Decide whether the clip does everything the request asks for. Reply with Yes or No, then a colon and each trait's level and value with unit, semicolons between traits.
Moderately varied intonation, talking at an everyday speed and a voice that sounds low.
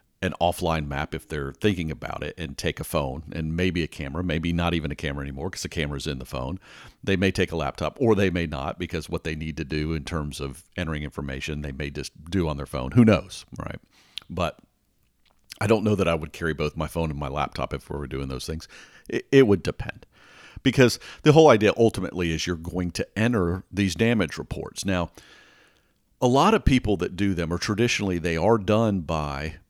No: average, 4.3 semitones; fast, 220 wpm; very low, 85 Hz